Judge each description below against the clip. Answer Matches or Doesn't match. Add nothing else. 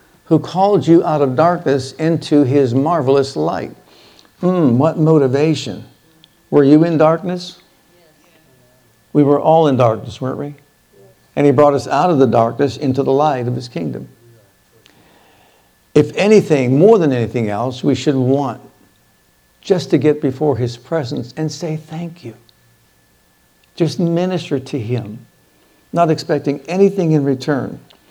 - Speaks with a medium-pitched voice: Matches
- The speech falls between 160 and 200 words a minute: Doesn't match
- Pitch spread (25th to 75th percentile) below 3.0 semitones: Doesn't match